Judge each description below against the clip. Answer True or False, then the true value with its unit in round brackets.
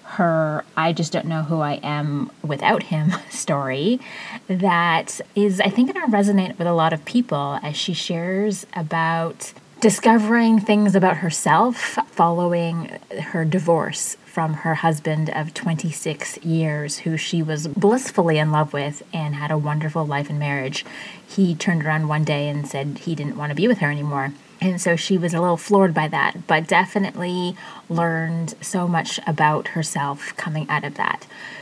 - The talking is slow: False (165 wpm)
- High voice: False (165 Hz)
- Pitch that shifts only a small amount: False (3.4 semitones)